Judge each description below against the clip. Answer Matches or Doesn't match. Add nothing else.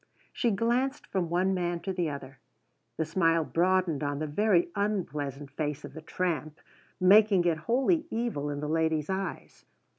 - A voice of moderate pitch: Matches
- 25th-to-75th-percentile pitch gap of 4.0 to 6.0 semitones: Matches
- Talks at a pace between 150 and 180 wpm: Matches